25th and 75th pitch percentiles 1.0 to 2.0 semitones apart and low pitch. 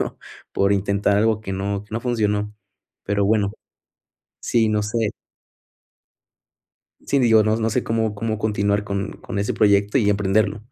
Yes: narrow, 1.5 semitones; low, 105 Hz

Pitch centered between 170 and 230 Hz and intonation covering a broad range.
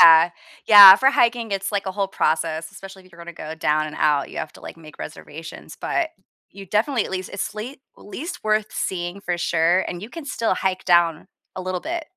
No: medium, 185 Hz; average, 4.3 semitones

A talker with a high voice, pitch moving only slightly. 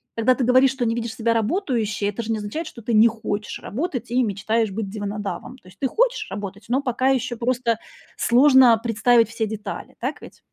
No: high, 230 Hz; average, 3.0 semitones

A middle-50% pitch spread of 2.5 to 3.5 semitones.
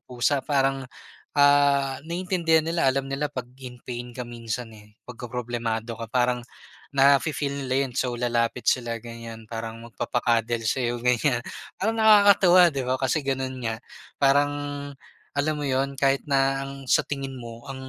Yes: average, 2.8 semitones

